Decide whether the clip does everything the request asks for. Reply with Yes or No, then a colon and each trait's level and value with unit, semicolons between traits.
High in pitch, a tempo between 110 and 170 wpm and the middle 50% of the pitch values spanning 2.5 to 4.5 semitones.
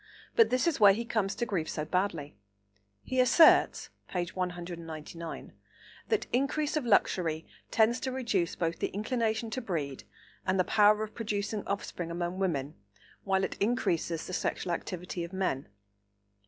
No: high, 195 Hz; average, 155 wpm; average, 5.1 semitones